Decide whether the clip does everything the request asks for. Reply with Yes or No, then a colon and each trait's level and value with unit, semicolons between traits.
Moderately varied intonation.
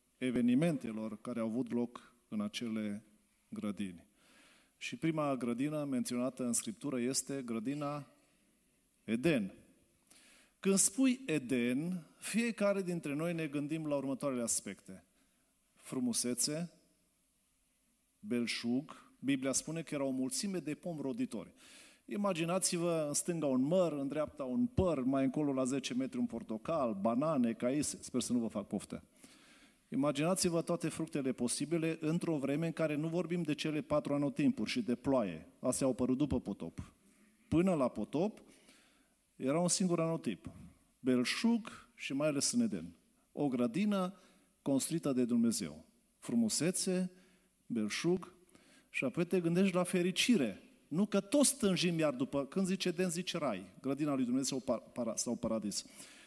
No: wide, 6.0 semitones